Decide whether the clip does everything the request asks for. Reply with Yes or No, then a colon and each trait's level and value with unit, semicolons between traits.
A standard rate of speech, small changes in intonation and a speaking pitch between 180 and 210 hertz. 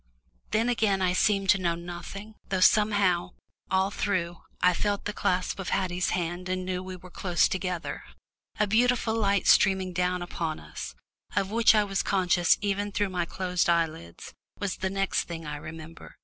Yes: average, 175 wpm; narrow, 2.3 semitones; medium, 185 Hz